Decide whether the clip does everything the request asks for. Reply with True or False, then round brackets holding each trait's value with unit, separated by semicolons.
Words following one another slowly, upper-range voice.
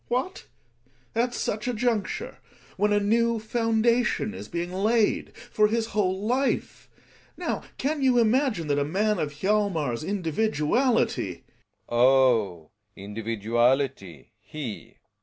True (130 wpm; 205 Hz)